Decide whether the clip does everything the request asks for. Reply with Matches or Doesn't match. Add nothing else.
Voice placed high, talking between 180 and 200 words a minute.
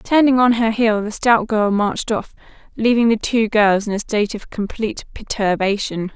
Matches